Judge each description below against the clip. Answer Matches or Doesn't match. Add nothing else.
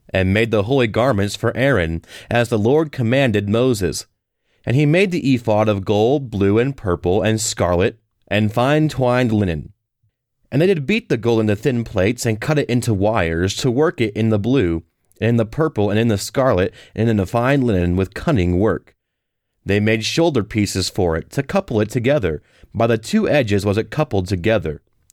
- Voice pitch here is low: Matches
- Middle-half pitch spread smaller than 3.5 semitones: Doesn't match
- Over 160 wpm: Matches